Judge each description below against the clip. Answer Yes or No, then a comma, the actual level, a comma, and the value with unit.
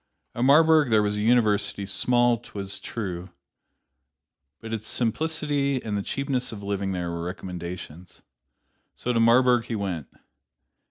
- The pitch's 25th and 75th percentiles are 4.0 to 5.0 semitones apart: Yes, average, 4.3 semitones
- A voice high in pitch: No, low, 110 Hz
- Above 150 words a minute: No, average, 145 wpm